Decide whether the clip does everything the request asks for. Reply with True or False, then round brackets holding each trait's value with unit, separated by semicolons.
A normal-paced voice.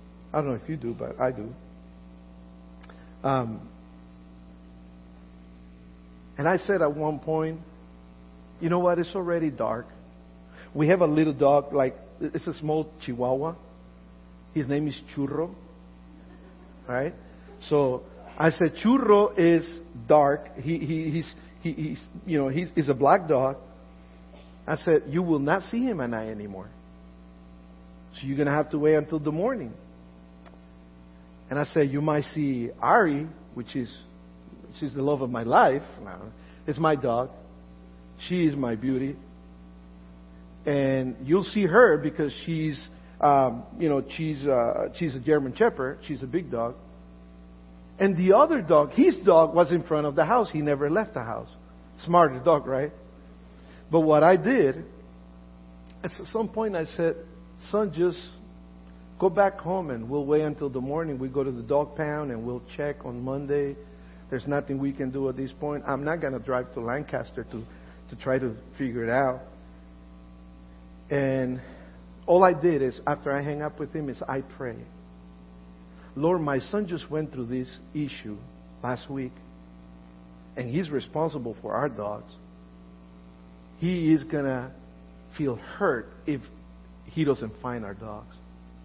True (155 wpm)